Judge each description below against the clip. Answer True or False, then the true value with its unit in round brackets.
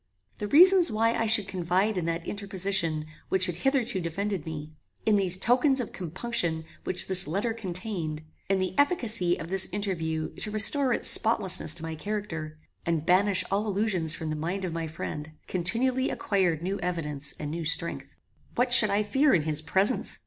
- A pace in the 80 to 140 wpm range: False (180 wpm)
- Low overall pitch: False (190 Hz)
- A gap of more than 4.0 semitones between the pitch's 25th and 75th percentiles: True (4.6 semitones)